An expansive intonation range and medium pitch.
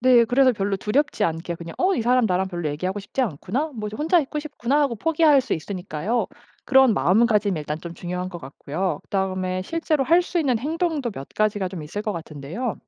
No: wide, 7.0 semitones; high, 210 Hz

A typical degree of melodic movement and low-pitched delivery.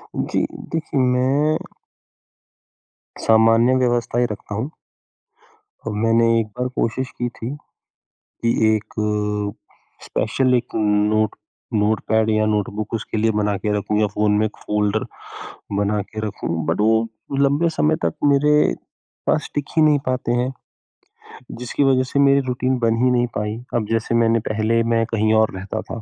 Yes: average, 3.0 semitones; low, 115 Hz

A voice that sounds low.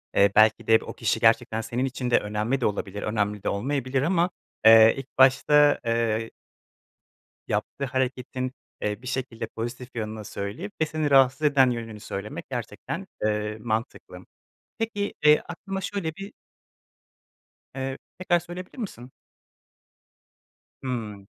Yes: low, 125 Hz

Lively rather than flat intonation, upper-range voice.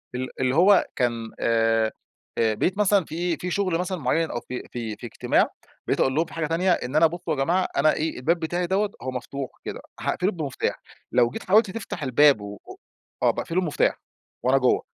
No: wide, 6.0 semitones; medium, 155 Hz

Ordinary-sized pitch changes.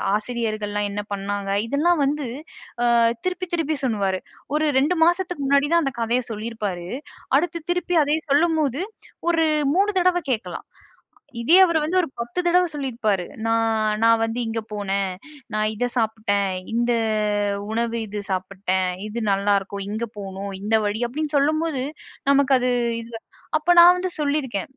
No: wide, 6.8 semitones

